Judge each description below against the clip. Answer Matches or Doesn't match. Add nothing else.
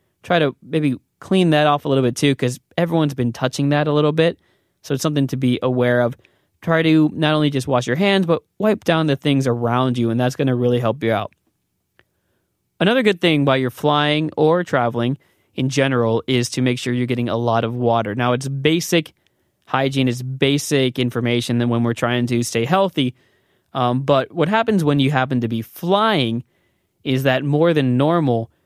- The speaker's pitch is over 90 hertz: Matches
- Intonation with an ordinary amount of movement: Matches